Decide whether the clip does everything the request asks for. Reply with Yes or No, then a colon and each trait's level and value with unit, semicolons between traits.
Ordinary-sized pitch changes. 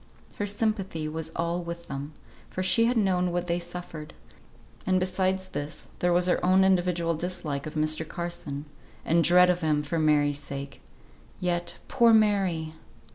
Yes: average, 3.0 semitones